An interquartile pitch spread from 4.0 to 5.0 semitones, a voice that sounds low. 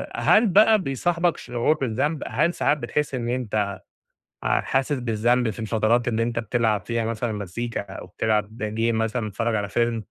No: average, 3.2 semitones; low, 120 Hz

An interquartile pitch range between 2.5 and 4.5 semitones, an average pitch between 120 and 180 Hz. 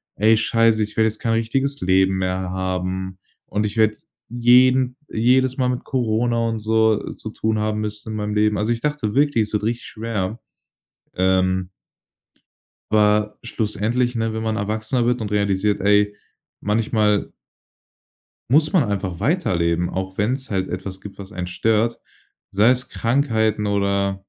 No: average, 2.8 semitones; low, 110 Hz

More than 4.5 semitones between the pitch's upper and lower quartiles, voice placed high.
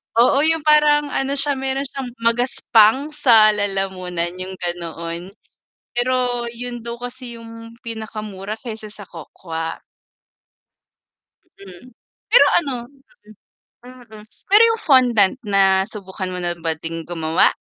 Yes: average, 5.2 semitones; high, 225 Hz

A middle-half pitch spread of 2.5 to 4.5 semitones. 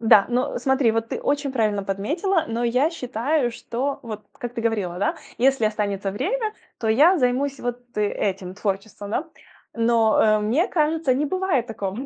No: average, 5.0 semitones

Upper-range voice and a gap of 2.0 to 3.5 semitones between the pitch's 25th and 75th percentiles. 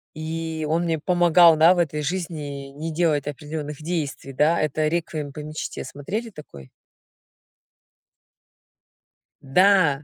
No: medium, 155 Hz; narrow, 2.5 semitones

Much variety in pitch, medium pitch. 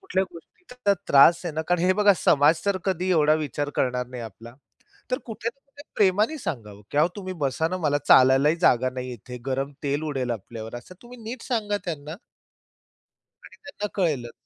Yes: wide, 7.7 semitones; medium, 155 Hz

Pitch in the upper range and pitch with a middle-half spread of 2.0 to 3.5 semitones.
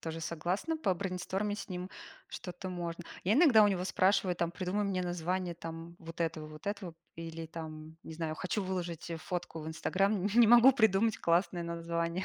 No: medium, 180 Hz; average, 2.8 semitones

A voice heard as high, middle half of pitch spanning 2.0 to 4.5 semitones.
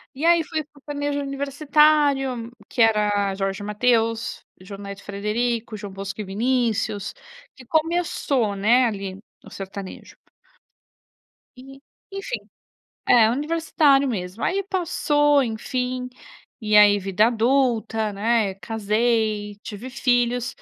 No: high, 230 Hz; average, 4.9 semitones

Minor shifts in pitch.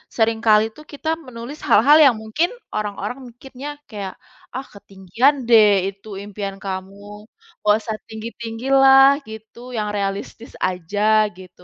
No: average, 3.6 semitones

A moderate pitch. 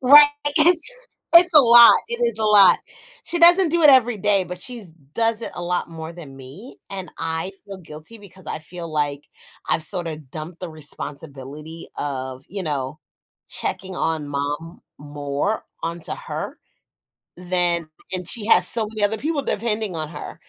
Yes: medium, 180 Hz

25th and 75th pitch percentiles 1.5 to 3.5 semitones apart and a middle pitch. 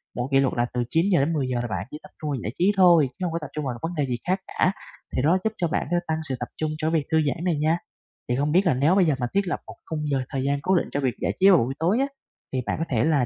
No: average, 4.8 semitones; medium, 155 Hz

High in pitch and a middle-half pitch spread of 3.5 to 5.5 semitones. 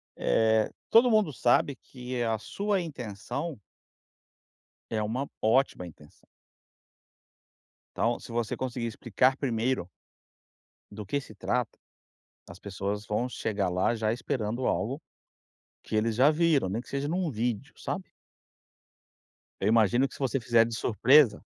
No: low, 120 Hz; average, 3.9 semitones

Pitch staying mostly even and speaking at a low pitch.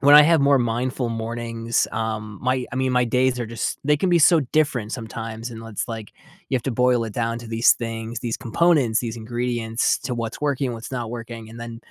Yes: narrow, 2.2 semitones; low, 120 Hz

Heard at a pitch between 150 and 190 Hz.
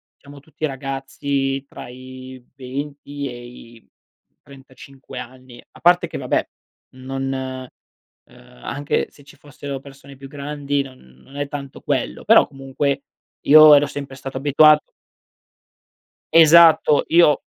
No: medium, 140 Hz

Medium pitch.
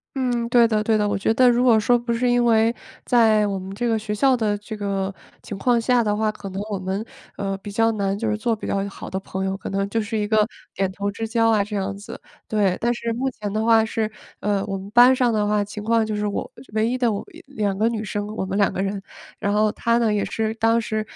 No: high, 215 Hz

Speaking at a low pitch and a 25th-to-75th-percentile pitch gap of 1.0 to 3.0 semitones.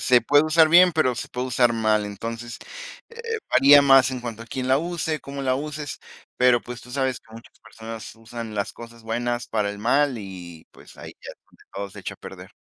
No: low, 120 Hz; average, 3.6 semitones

